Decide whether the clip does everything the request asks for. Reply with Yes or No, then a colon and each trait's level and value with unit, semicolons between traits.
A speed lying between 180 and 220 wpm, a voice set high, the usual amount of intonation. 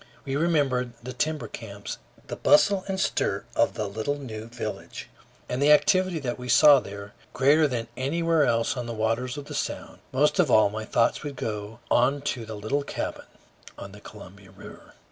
No: average, 185 wpm; low, 125 Hz; average, 4.9 semitones